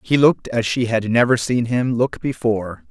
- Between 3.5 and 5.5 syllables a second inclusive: Yes, 5.1 syllables/s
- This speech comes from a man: Yes, male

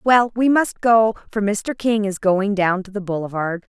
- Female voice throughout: Yes, female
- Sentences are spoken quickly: Yes, fast, 210 wpm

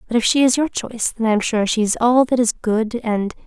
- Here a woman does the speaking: Yes, female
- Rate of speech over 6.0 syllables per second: No, 4.8 syllables/s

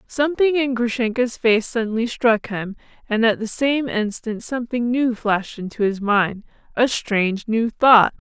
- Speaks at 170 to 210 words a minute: No, average, 160 wpm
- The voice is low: No, high, 230 Hz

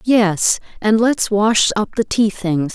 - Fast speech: No, average, 175 wpm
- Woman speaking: Yes, female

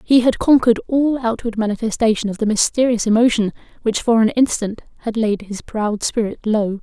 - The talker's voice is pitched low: No, high, 225 Hz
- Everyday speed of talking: Yes, average, 175 wpm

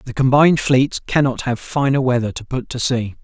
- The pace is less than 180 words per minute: No, fast, 205 wpm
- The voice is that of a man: Yes, male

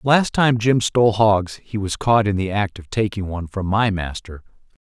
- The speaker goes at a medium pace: No, fast, 235 wpm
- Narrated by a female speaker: No, male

